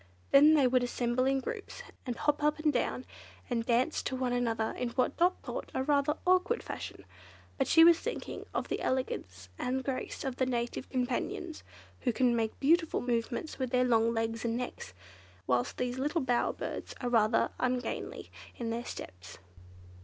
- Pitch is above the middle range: Yes, very high, 255 Hz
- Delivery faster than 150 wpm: Yes, average, 175 wpm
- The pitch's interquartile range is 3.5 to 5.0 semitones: No, average, 3.1 semitones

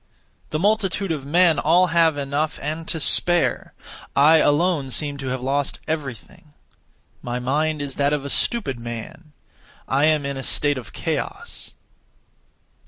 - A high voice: No, medium, 150 Hz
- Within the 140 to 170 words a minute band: Yes, average, 150 wpm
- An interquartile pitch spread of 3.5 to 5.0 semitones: No, average, 2.8 semitones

